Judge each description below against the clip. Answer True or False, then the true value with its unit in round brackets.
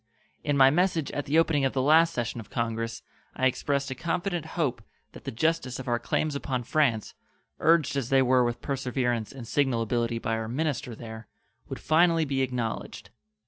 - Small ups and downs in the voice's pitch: False (4.3 semitones)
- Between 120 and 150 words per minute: False (185 wpm)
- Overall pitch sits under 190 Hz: True (135 Hz)